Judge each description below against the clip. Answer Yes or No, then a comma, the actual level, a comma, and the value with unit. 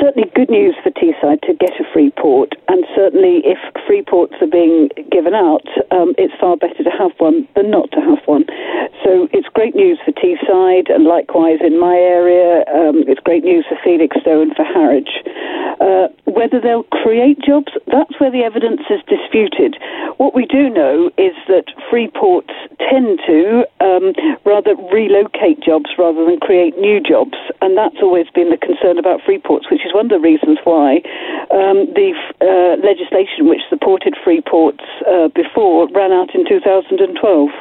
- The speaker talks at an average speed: Yes, average, 170 wpm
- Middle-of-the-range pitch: No, very high, 285 Hz